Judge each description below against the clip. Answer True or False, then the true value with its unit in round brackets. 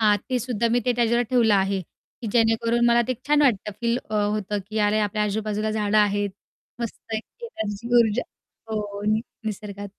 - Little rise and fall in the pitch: True (2.3 semitones)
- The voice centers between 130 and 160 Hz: False (215 Hz)